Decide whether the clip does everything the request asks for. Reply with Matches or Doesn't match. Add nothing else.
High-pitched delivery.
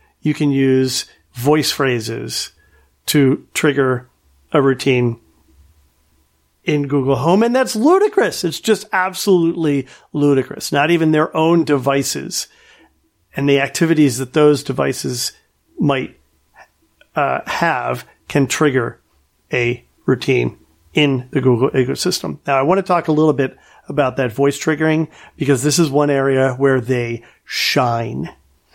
Doesn't match